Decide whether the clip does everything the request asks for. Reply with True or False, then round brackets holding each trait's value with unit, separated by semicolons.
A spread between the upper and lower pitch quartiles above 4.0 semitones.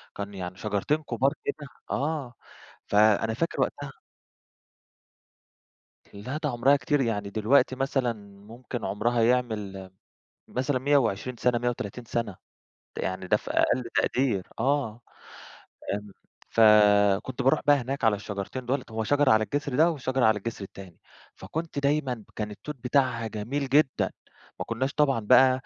True (4.4 semitones)